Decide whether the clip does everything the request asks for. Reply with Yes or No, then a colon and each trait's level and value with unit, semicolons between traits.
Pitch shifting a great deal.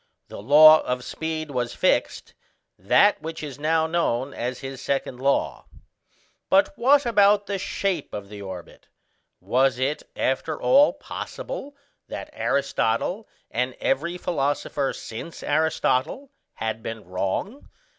Yes: wide, 6.2 semitones